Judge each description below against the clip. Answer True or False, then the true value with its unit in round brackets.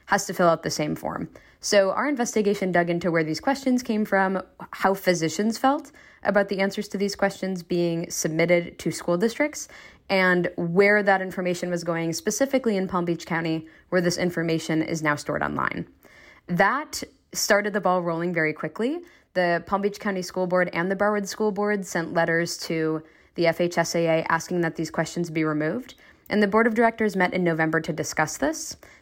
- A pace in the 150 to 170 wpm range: False (185 wpm)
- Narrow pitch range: False (3.7 semitones)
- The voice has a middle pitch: True (180 Hz)